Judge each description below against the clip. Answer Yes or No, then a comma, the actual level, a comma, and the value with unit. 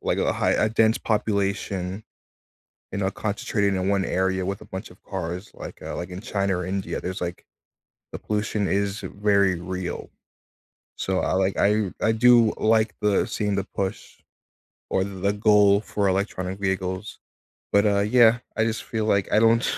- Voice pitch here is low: Yes, low, 100 Hz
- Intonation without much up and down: Yes, narrow, 2.1 semitones